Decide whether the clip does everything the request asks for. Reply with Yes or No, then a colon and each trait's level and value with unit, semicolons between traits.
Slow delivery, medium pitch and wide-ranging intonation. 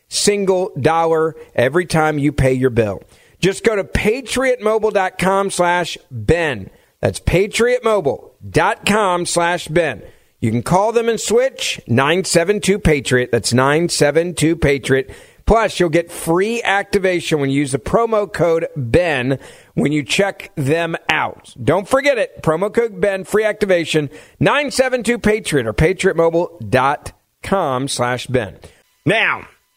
Yes: slow, 125 wpm; medium, 170 Hz; wide, 6.3 semitones